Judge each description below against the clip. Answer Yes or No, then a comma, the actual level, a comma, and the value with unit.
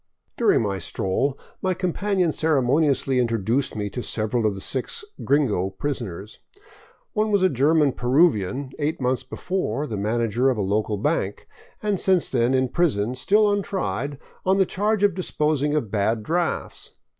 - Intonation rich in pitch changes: Yes, wide, 7.6 semitones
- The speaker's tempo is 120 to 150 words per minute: No, average, 160 wpm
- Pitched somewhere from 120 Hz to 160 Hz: Yes, low, 135 Hz